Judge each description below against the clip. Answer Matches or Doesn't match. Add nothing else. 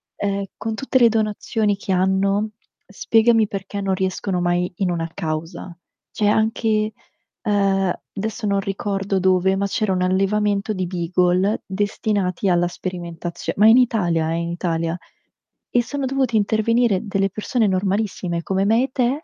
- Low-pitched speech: Doesn't match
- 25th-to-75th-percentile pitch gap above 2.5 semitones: Matches